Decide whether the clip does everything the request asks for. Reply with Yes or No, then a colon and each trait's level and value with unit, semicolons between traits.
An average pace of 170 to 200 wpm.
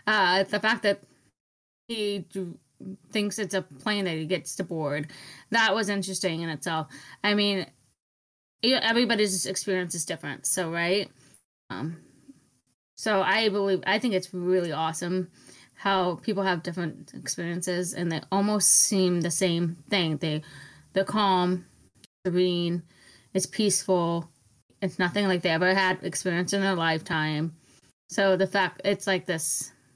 No: average, 140 wpm